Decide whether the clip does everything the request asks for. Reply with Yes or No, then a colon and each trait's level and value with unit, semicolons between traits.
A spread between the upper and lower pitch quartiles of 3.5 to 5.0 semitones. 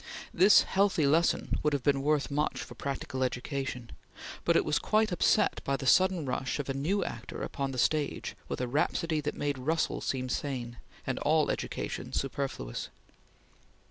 No: average, 3.0 semitones